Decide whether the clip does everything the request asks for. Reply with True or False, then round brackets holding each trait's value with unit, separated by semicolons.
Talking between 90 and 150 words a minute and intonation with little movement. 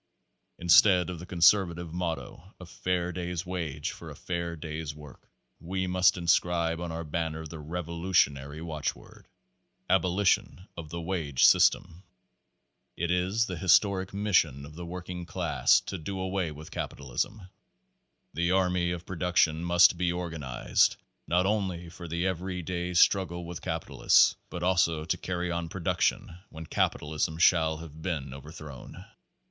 True (145 wpm; 2.2 semitones)